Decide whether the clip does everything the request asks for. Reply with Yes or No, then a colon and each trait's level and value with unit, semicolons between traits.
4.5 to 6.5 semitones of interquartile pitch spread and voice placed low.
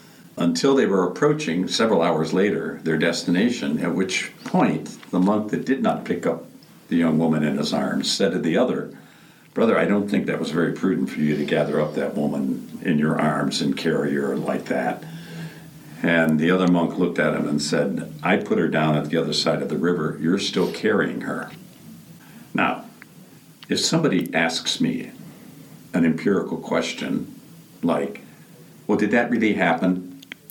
Yes: average, 4.8 semitones; very low, 90 Hz